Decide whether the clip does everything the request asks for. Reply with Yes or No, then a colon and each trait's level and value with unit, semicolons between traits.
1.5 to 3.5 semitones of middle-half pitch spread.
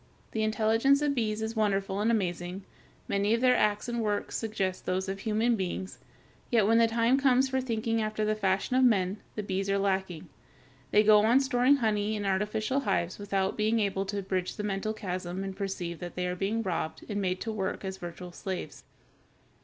Yes: average, 2.9 semitones